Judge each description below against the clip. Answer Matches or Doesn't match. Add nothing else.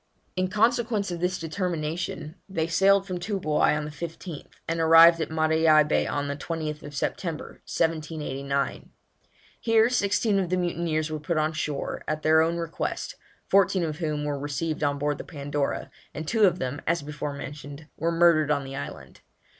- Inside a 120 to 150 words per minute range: Doesn't match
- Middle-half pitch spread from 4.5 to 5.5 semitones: Doesn't match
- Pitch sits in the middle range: Matches